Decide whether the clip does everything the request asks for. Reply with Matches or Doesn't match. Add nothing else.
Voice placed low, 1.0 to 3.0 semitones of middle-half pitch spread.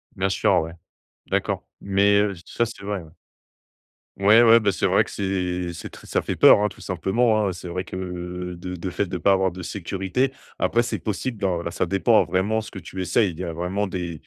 Matches